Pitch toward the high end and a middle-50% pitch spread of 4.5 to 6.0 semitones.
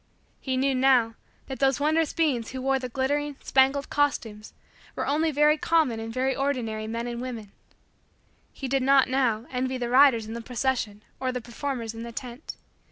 No: very high, 260 Hz; average, 2.9 semitones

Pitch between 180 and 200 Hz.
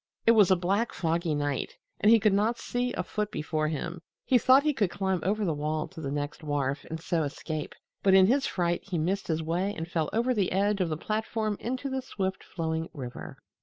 Yes: medium, 185 Hz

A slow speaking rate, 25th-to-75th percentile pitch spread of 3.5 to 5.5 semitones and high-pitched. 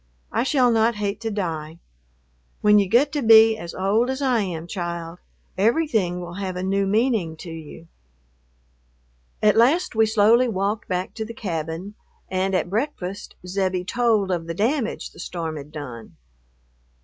No: average, 160 wpm; average, 4.5 semitones; high, 200 Hz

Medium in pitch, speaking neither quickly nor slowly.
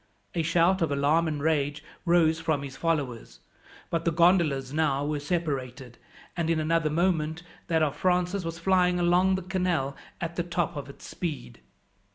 Yes: medium, 165 Hz; average, 170 wpm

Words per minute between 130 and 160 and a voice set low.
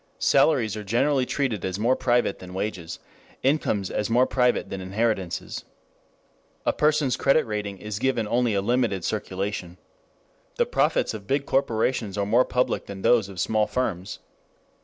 Yes: average, 155 wpm; low, 110 Hz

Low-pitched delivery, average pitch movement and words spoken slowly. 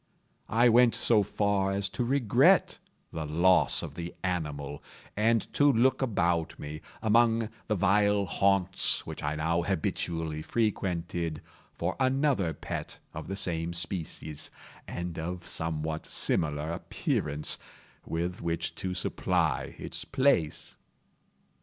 Yes: very low, 90 Hz; average, 4.6 semitones; slow, 120 wpm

